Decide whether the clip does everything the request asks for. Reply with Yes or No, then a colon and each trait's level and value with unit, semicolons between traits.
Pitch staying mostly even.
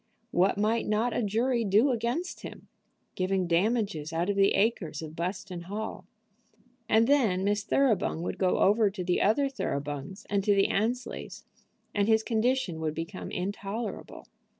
No: average, 3.8 semitones